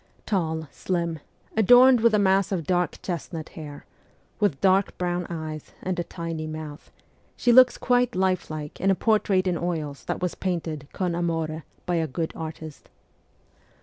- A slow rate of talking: No, average, 155 wpm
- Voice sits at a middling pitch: Yes, medium, 175 Hz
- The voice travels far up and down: No, average, 3.2 semitones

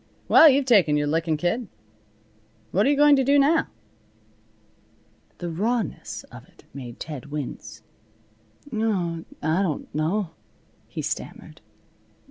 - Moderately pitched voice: Yes, medium, 180 Hz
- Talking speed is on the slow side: Yes, slow, 120 wpm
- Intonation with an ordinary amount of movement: No, wide, 7.9 semitones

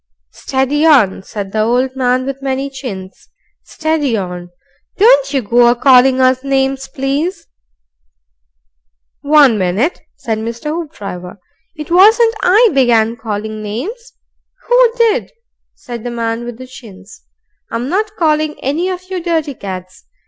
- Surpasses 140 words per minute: No, slow, 135 wpm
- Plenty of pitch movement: Yes, wide, 5.7 semitones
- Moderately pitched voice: No, very high, 265 Hz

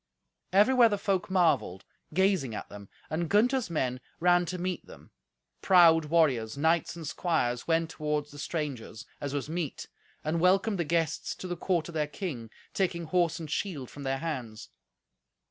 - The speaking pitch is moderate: Yes, medium, 165 Hz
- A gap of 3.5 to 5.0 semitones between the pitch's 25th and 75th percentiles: Yes, average, 3.8 semitones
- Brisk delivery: No, average, 165 wpm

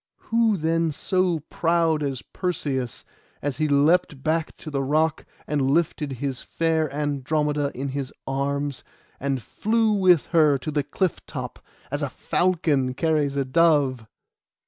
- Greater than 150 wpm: No, average, 145 wpm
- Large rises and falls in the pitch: No, average, 3.1 semitones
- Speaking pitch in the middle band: Yes, medium, 150 Hz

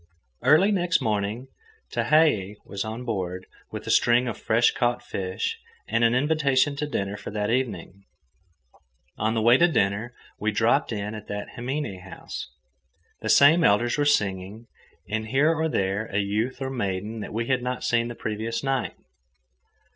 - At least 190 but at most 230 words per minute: No, average, 165 wpm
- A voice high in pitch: No, low, 115 Hz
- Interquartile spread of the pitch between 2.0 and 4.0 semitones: No, average, 4.4 semitones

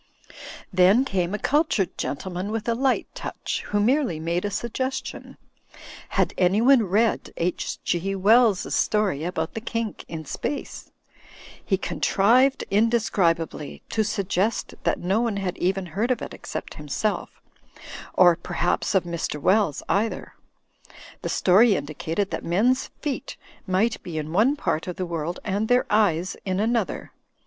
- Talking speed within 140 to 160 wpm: Yes, average, 145 wpm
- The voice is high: Yes, high, 200 Hz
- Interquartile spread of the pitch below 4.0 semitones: No, average, 4.4 semitones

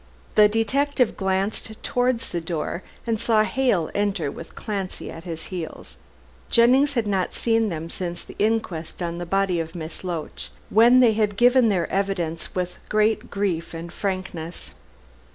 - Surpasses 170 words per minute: No, average, 155 wpm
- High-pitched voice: Yes, high, 195 Hz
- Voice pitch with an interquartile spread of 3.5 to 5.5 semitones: Yes, average, 4.7 semitones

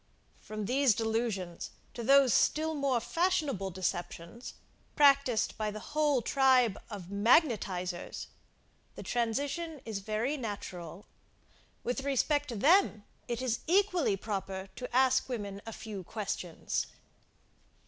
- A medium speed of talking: No, slow, 115 wpm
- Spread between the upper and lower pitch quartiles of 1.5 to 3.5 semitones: No, wide, 5.6 semitones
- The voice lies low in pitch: No, high, 235 Hz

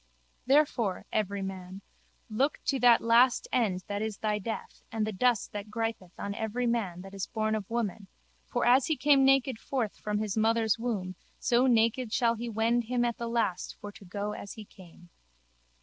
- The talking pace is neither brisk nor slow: Yes, average, 185 wpm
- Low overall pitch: No, high, 220 Hz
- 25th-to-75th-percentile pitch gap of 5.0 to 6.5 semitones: No, average, 2.9 semitones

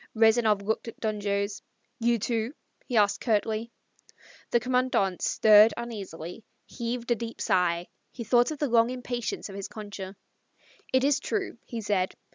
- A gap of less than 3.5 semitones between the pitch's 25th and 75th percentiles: Yes, average, 2.9 semitones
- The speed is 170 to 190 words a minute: No, average, 155 wpm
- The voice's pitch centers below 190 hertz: No, high, 225 Hz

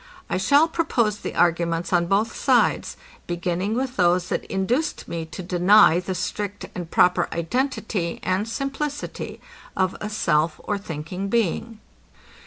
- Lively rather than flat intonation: No, average, 4.5 semitones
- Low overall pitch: No, high, 190 Hz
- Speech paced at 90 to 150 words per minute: Yes, average, 140 wpm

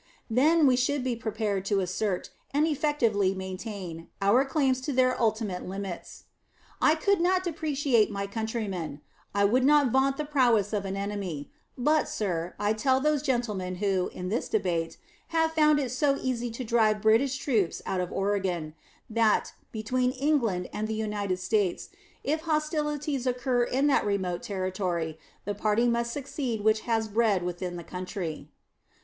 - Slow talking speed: No, average, 160 wpm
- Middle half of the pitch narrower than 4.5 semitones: No, wide, 5.6 semitones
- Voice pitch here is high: Yes, high, 220 Hz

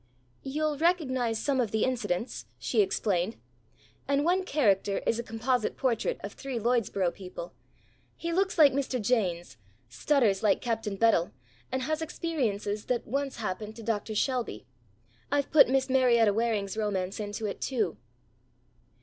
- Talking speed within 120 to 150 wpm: Yes, average, 145 wpm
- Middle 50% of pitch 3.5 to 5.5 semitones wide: Yes, average, 4.8 semitones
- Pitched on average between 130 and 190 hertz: No, high, 230 Hz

